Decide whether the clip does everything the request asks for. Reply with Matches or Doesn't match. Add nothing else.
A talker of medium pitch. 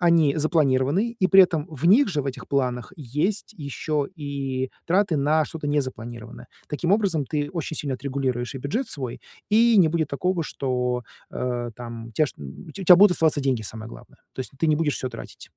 Matches